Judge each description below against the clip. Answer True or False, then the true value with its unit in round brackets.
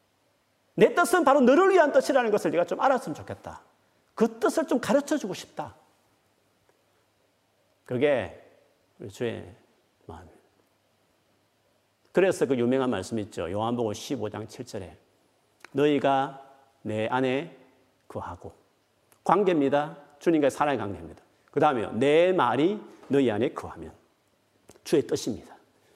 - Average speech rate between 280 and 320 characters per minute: False (260 characters per minute)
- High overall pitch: False (140 Hz)